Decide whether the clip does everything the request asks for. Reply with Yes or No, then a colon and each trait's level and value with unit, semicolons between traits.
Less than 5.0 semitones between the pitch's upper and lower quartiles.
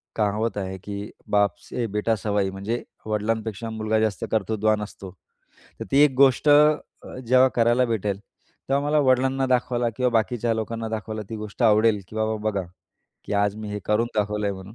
Yes: narrow, 2.4 semitones